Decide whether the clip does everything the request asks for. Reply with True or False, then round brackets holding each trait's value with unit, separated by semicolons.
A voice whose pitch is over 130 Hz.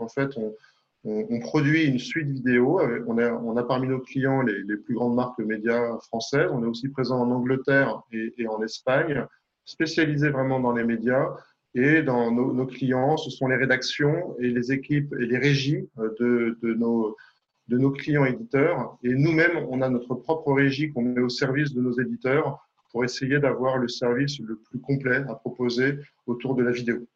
False (125 Hz)